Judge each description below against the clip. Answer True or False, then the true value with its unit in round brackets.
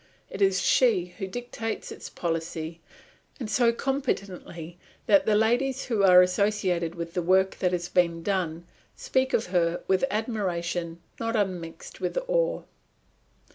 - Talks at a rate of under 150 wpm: True (140 wpm)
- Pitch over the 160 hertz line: True (190 Hz)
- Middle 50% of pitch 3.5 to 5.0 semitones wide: True (4.7 semitones)